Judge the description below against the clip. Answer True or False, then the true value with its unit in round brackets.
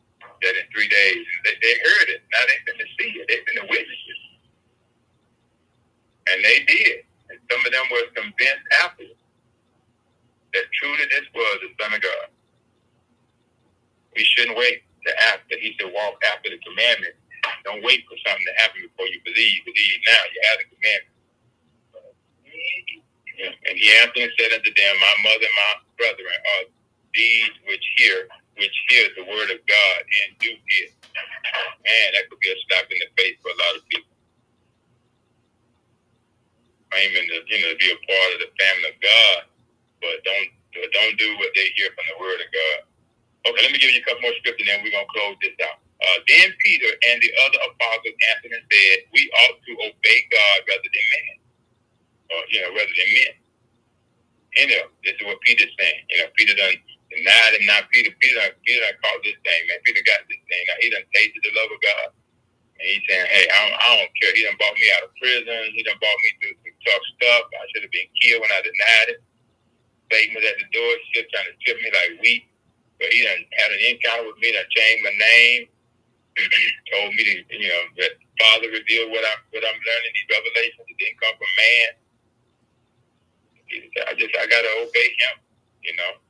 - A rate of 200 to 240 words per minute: True (205 wpm)